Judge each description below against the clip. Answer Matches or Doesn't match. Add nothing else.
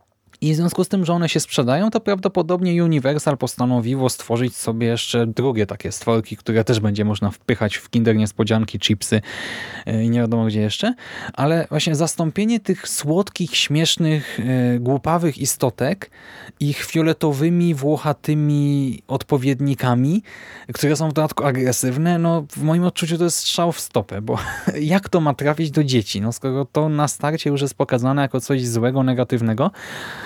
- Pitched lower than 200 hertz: Matches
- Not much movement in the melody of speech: Doesn't match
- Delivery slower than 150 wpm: Doesn't match